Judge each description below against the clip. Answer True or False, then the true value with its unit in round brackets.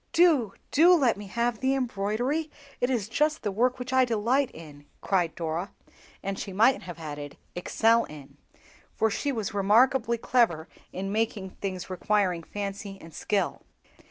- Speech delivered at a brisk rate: False (155 wpm)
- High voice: True (210 Hz)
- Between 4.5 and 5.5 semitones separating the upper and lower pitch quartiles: True (5.1 semitones)